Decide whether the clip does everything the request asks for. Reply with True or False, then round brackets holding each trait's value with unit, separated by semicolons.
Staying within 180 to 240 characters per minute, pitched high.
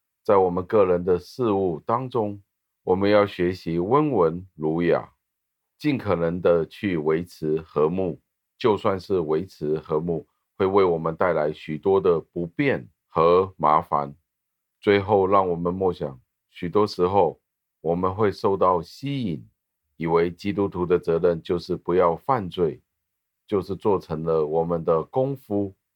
False (210 characters per minute; 85 Hz)